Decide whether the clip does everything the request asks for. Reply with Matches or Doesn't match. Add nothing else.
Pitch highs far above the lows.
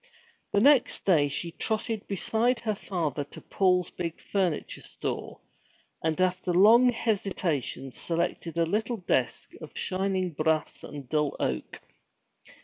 Doesn't match